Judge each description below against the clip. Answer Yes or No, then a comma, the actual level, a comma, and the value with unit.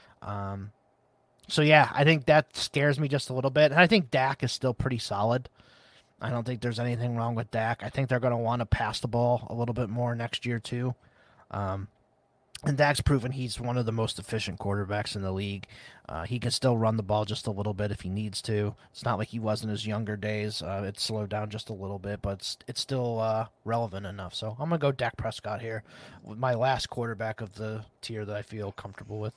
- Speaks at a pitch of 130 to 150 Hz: No, low, 115 Hz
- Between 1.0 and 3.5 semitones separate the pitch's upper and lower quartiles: Yes, average, 3.1 semitones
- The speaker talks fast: Yes, fast, 240 wpm